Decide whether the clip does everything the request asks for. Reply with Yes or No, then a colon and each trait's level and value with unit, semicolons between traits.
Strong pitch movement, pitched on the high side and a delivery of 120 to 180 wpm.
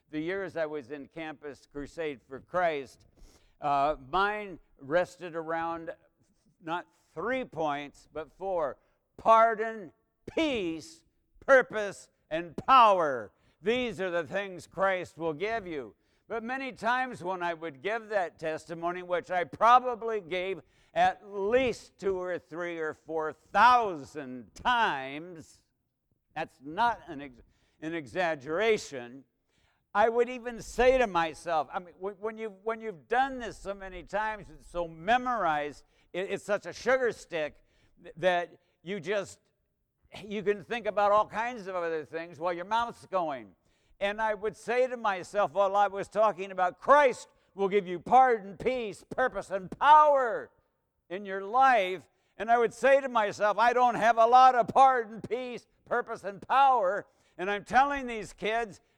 Yes: wide, 5.7 semitones; high, 195 Hz; average, 150 wpm